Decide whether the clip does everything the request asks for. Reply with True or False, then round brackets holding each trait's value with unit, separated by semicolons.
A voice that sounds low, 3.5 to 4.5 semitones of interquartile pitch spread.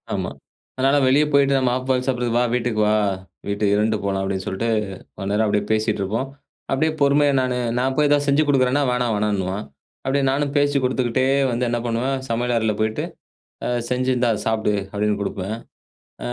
True (120 Hz; 4.0 semitones)